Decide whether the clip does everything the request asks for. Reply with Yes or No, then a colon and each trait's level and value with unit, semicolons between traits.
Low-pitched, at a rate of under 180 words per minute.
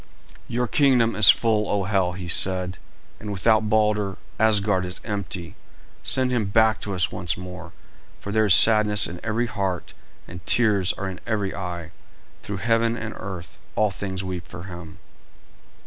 Yes: low, 100 Hz; average, 165 wpm